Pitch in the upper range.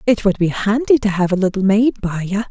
Yes: high, 205 Hz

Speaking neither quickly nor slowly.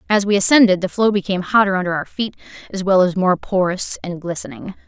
No: fast, 210 wpm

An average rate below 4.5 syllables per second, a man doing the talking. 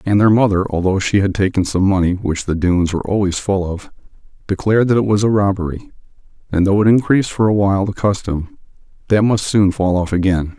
Yes: 4.2 syllables/s; male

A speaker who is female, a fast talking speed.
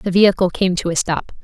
Yes: female; fast, 250 wpm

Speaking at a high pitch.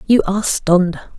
Yes: high, 195 Hz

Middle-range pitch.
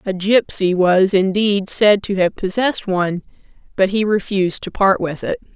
No: high, 195 Hz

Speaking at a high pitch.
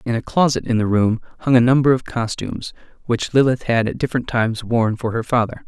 No: low, 120 Hz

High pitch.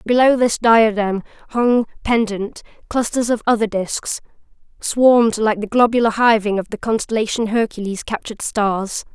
Yes: high, 220 Hz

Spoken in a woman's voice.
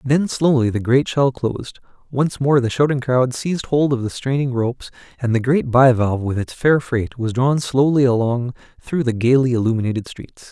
No: male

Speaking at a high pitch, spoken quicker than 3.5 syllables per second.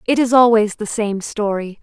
Yes: high, 220 Hz; 4.8 syllables/s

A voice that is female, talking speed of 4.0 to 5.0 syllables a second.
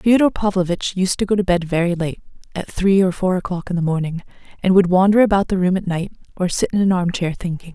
No: female; 6.2 syllables/s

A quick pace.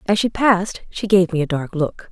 Yes: fast, 255 wpm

